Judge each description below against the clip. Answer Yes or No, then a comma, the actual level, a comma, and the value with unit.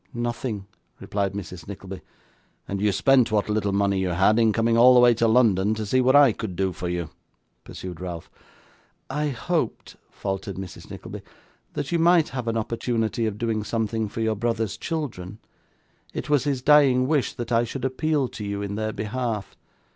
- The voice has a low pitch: Yes, low, 110 Hz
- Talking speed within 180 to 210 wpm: Yes, average, 185 wpm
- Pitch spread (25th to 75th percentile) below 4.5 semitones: Yes, average, 4.0 semitones